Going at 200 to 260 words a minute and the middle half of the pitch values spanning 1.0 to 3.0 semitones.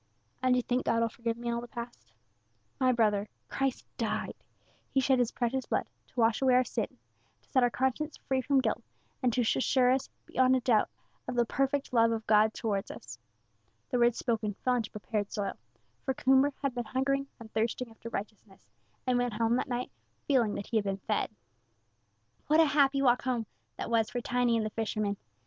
Yes: fast, 205 wpm; narrow, 2.6 semitones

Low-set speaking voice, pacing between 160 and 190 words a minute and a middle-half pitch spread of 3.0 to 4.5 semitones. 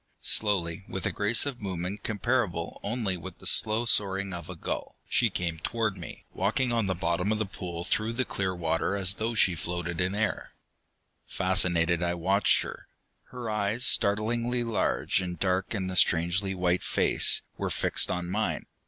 Yes: very low, 95 Hz; average, 175 wpm; average, 3.7 semitones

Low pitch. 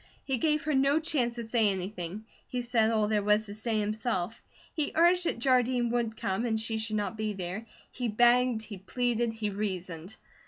No: high, 225 Hz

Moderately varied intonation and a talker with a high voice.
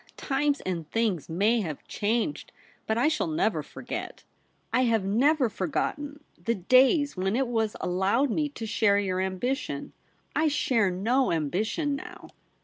No: wide, 6.7 semitones; high, 230 Hz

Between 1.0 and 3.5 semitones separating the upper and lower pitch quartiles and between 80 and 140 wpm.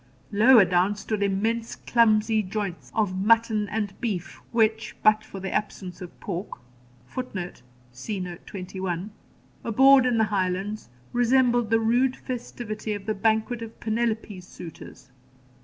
Yes: average, 3.1 semitones; slow, 135 wpm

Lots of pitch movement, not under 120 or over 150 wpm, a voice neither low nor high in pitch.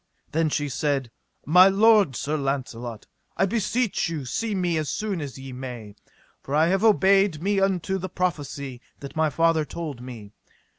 No: wide, 6.1 semitones; average, 165 wpm; medium, 155 Hz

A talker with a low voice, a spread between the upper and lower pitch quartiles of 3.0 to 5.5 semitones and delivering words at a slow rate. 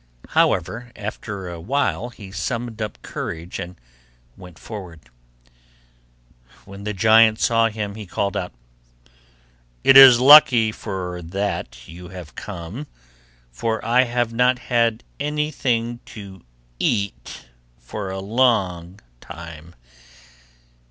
Yes: low, 105 Hz; average, 4.7 semitones; slow, 110 wpm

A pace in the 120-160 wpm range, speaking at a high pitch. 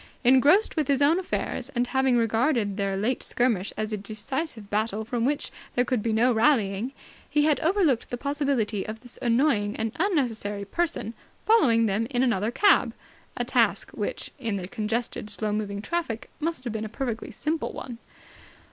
No: average, 175 wpm; high, 235 Hz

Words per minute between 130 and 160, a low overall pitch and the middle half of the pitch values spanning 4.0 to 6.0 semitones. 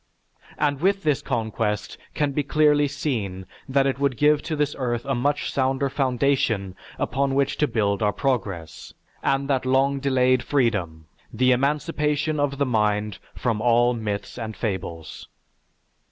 Yes: average, 150 wpm; low, 130 Hz; average, 4.3 semitones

